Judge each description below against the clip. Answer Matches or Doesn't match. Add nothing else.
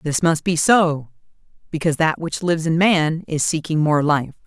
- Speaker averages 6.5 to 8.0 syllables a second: Doesn't match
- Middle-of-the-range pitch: Matches